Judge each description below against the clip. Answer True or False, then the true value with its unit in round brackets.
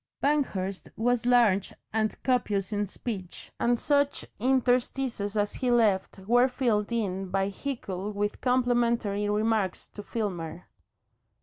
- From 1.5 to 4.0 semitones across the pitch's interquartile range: True (3.7 semitones)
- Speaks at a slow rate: True (120 wpm)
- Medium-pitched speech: False (220 Hz)